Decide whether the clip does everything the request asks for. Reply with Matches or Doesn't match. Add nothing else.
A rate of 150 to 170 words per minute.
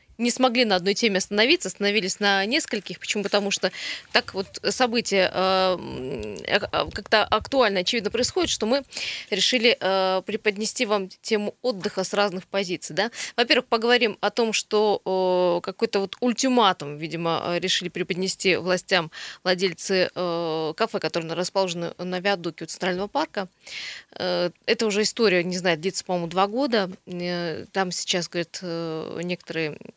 Doesn't match